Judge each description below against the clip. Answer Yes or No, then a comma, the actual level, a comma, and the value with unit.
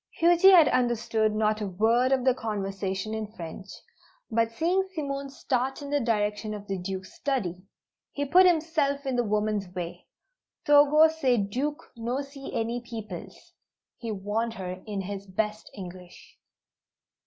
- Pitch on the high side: Yes, high, 225 Hz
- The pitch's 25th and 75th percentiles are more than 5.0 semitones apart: Yes, wide, 5.4 semitones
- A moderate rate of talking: Yes, average, 150 wpm